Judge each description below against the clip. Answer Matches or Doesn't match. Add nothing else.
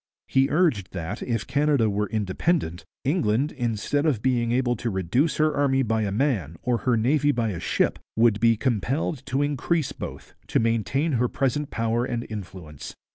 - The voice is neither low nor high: Doesn't match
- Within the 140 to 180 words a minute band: Matches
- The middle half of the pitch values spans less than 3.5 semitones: Doesn't match